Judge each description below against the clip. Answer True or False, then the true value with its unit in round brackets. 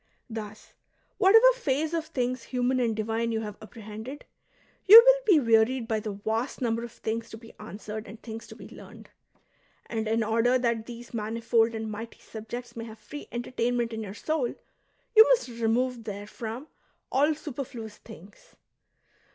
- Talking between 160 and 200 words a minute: True (165 wpm)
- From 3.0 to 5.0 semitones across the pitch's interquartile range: False (2.5 semitones)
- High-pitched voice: True (230 Hz)